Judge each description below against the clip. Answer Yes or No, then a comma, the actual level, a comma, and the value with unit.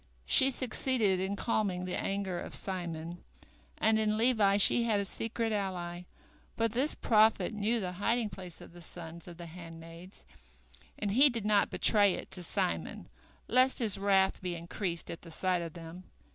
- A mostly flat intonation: No, average, 4.0 semitones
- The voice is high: Yes, high, 195 Hz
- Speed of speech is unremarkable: Yes, average, 175 wpm